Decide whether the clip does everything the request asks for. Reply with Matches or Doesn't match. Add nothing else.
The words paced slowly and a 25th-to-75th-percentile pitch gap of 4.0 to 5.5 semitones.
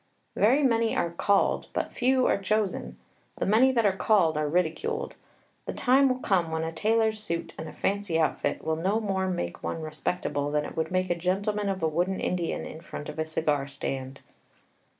Doesn't match